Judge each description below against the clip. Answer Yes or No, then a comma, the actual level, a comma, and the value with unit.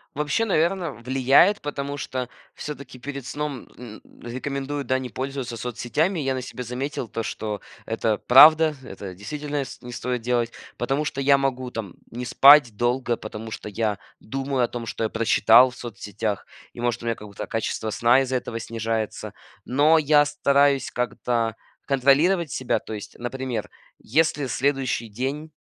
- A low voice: Yes, low, 130 Hz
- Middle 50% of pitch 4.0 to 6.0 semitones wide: No, average, 3.5 semitones